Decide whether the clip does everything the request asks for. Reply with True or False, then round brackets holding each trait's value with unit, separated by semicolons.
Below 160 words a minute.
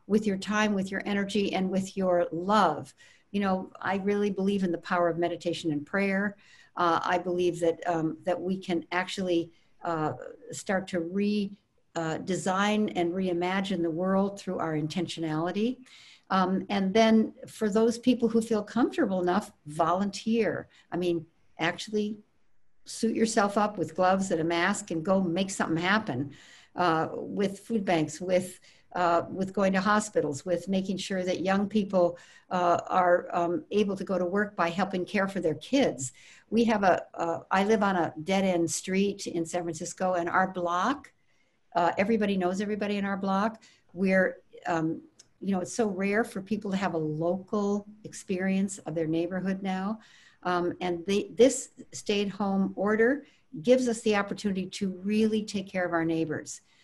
False (170 wpm)